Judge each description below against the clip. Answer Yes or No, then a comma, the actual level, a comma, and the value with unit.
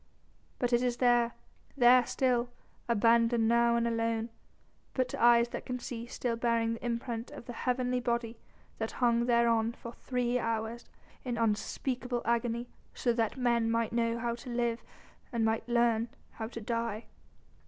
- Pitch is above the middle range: Yes, high, 235 Hz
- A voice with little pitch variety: Yes, narrow, 1.0 semitones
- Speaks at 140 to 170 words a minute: Yes, average, 160 wpm